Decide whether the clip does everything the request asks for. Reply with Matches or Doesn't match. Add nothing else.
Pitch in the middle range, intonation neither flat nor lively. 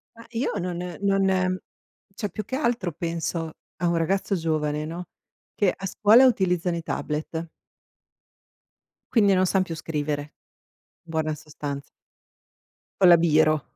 Matches